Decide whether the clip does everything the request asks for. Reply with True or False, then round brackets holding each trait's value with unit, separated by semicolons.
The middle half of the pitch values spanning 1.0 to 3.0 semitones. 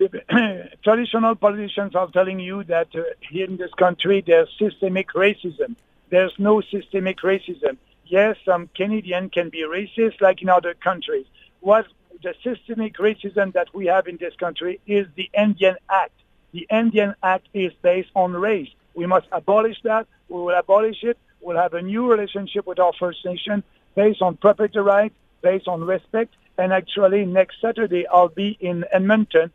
True (2.7 semitones)